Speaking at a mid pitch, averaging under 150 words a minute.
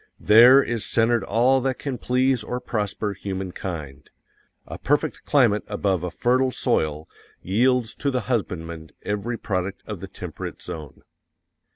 No: low, 110 Hz; average, 140 wpm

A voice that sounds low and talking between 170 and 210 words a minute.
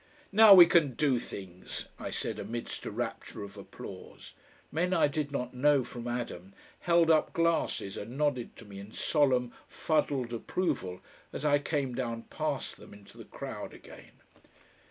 No: low, 130 Hz; average, 160 wpm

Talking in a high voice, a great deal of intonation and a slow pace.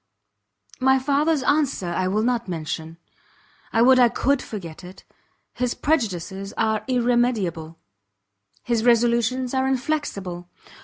Yes: high, 235 Hz; wide, 5.8 semitones; slow, 115 wpm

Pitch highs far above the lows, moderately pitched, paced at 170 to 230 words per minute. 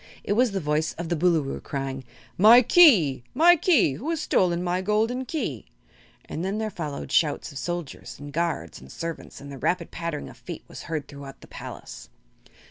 Yes: wide, 6.8 semitones; medium, 170 Hz; average, 190 wpm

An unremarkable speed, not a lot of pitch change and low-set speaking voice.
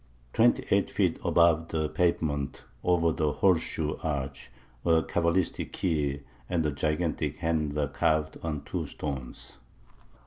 No: slow, 130 wpm; narrow, 2.3 semitones; very low, 80 Hz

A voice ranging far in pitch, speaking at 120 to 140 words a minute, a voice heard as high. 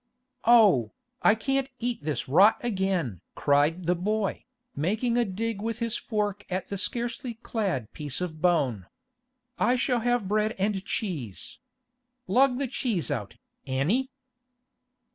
Yes: wide, 6.0 semitones; slow, 135 wpm; high, 205 Hz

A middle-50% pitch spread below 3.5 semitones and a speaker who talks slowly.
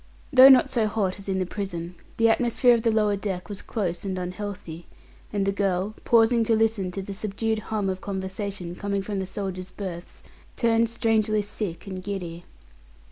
No: average, 2.9 semitones; average, 185 wpm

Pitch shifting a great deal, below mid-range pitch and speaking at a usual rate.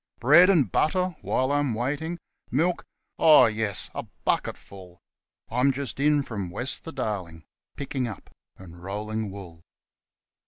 Yes: wide, 6.6 semitones; low, 125 Hz; average, 145 wpm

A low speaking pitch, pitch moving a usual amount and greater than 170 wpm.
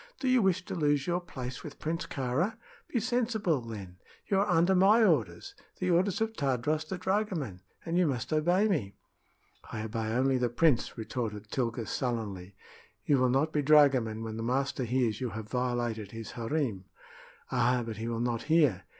No: low, 130 Hz; wide, 6.8 semitones; average, 180 wpm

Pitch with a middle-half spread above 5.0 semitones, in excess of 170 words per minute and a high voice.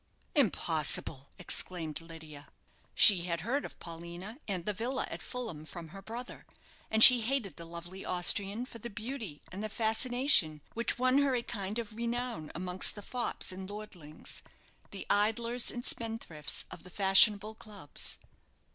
No: wide, 5.4 semitones; average, 155 wpm; high, 205 Hz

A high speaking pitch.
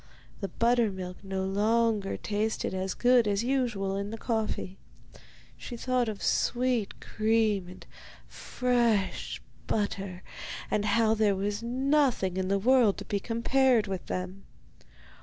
Yes: high, 215 Hz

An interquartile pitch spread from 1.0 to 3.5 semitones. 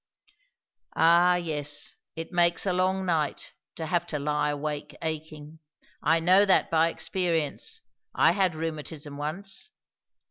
Yes: average, 3.0 semitones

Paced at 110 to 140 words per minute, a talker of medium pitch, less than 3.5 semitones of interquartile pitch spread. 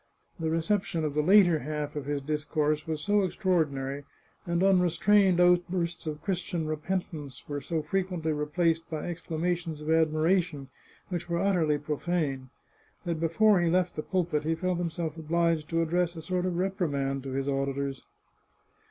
No: average, 160 wpm; medium, 165 Hz; average, 2.9 semitones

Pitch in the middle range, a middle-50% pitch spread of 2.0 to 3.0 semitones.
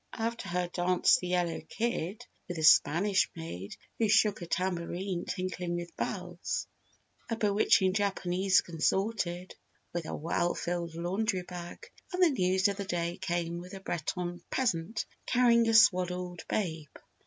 Yes: medium, 180 Hz; average, 2.7 semitones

